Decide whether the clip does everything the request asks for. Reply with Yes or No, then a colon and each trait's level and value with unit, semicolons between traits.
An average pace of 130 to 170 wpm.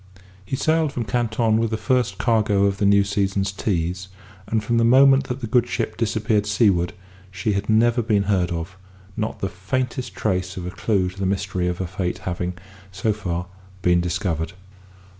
No: average, 185 wpm